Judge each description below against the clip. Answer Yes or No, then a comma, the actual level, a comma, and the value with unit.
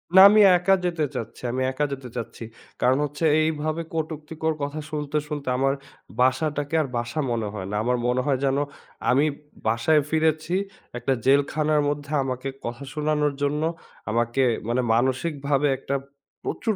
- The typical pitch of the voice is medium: Yes, medium, 145 Hz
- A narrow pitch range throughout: No, average, 3.2 semitones